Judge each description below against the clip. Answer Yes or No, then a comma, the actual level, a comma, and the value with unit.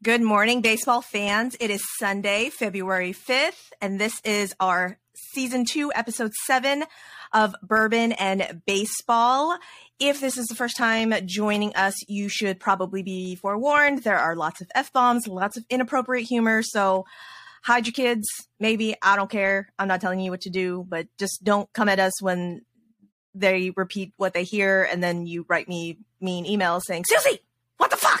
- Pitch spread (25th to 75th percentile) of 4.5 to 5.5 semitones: No, average, 3.8 semitones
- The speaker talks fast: No, average, 175 wpm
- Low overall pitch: No, high, 205 Hz